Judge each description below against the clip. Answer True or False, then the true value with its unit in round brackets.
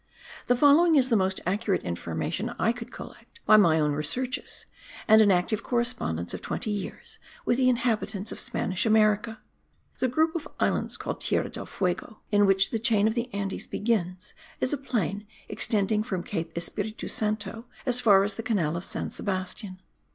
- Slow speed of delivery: False (175 wpm)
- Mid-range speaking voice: False (215 Hz)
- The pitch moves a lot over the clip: False (4.0 semitones)